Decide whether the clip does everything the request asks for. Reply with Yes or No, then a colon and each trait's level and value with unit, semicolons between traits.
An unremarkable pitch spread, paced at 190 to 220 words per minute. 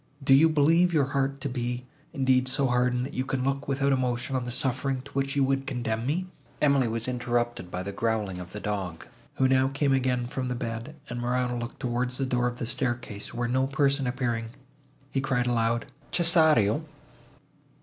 No: narrow, 2.3 semitones; average, 195 wpm